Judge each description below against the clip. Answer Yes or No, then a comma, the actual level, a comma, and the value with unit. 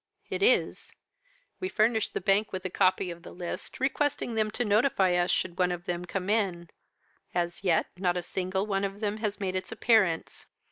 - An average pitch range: Yes, average, 3.4 semitones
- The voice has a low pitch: No, high, 190 Hz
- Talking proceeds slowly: No, average, 195 wpm